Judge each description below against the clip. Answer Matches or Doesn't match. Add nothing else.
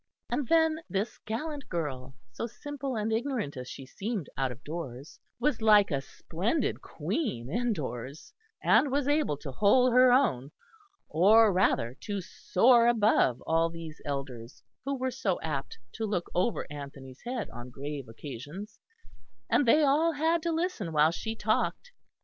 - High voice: Matches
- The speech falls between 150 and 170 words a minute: Matches